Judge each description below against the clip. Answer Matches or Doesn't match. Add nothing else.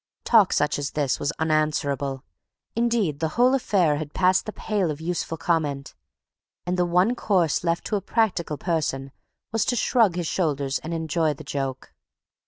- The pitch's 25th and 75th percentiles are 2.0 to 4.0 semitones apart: Doesn't match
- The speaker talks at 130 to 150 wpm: Doesn't match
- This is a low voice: Doesn't match